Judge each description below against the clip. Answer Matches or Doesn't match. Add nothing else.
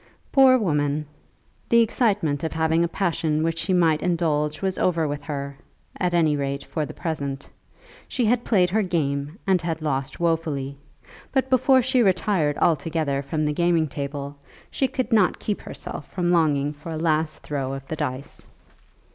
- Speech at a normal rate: Matches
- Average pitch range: Matches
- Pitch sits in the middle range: Matches